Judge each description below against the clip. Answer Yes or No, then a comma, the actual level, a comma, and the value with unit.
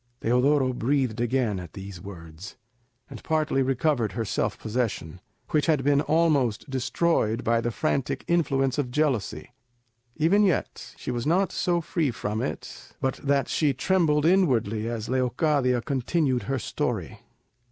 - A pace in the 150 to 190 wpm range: No, average, 140 wpm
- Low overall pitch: Yes, low, 130 Hz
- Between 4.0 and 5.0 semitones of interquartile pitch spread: Yes, average, 4.7 semitones